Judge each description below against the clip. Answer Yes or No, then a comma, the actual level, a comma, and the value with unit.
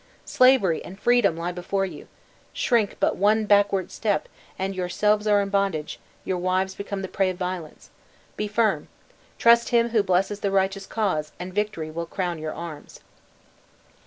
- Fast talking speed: No, average, 160 wpm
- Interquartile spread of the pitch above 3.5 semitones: No, average, 2.7 semitones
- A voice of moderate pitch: No, high, 195 Hz